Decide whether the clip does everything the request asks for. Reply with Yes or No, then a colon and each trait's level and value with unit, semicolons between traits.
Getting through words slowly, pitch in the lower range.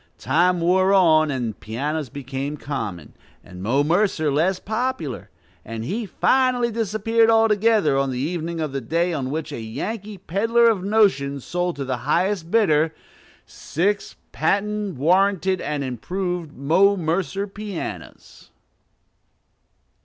No: slow, 130 wpm; medium, 170 Hz